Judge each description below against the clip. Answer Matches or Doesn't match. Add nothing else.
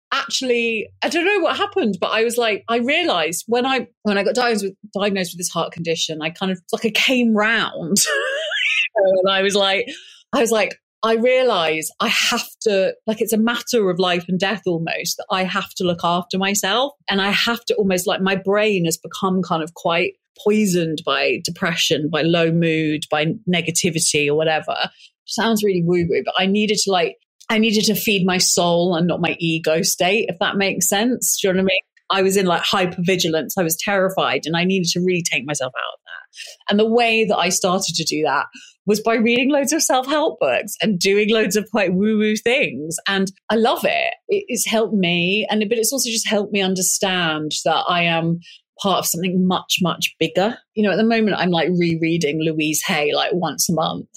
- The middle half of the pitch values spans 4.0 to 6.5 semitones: Matches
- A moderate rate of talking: Doesn't match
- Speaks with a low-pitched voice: Doesn't match